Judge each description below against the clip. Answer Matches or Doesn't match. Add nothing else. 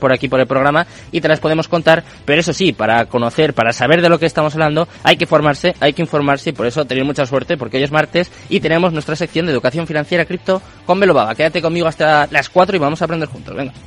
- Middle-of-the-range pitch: Matches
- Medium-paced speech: Doesn't match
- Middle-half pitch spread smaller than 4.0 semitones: Matches